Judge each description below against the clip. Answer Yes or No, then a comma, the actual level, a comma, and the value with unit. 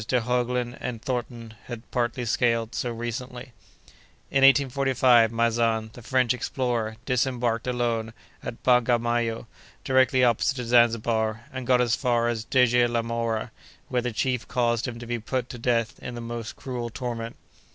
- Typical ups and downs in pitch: No, narrow, 1.3 semitones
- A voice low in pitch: Yes, low, 120 Hz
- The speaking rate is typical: Yes, average, 155 wpm